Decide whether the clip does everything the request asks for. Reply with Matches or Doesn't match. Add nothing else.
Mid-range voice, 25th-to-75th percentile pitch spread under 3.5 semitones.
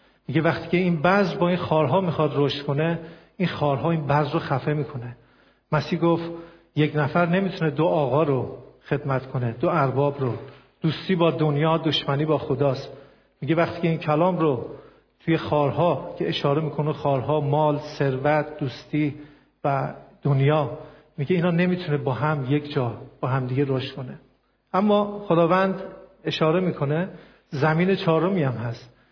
Matches